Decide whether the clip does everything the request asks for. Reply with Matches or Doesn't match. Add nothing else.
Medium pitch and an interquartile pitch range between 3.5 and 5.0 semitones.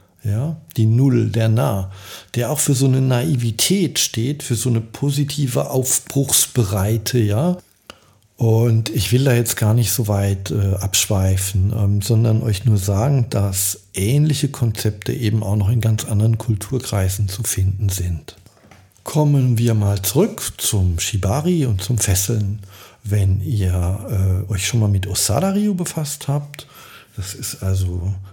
Doesn't match